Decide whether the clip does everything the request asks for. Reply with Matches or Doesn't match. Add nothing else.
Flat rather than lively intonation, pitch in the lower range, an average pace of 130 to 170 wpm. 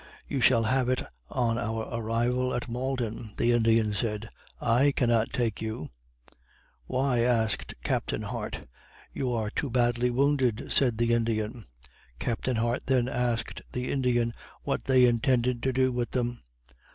Matches